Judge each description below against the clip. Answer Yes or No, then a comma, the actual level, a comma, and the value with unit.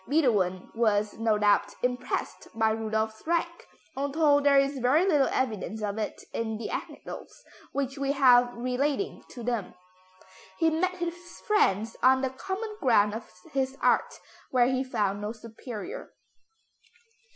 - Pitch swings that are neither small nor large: Yes, average, 4.6 semitones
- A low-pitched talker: No, very high, 250 Hz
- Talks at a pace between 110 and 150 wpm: Yes, average, 140 wpm